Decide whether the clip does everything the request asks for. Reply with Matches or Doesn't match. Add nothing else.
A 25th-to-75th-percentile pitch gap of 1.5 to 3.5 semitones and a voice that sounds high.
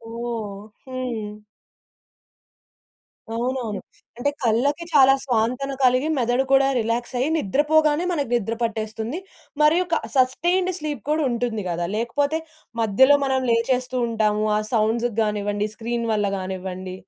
Doesn't match